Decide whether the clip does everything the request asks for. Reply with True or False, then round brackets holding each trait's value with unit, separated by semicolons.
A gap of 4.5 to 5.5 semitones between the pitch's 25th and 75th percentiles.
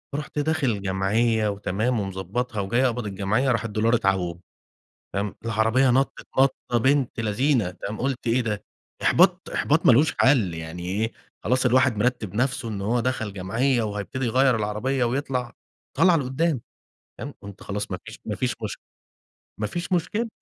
False (4.1 semitones)